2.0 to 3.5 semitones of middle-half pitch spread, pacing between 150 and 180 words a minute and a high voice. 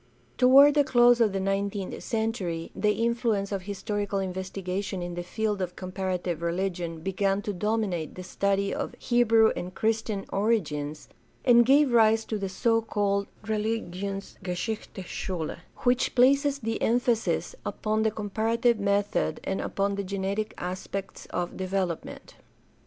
No: average, 3.1 semitones; slow, 135 wpm; high, 200 Hz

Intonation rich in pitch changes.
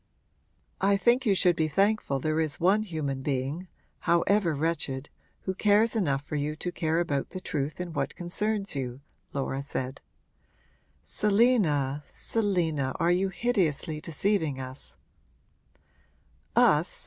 Yes: wide, 5.7 semitones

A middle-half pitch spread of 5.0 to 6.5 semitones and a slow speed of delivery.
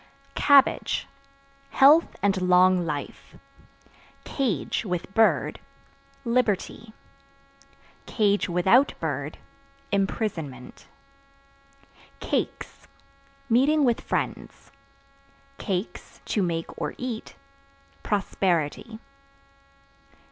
Yes: wide, 5.5 semitones; slow, 65 wpm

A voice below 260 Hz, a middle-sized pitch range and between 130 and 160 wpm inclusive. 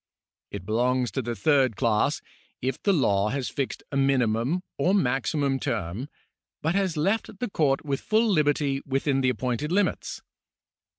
Yes: low, 135 Hz; average, 4.0 semitones; average, 155 wpm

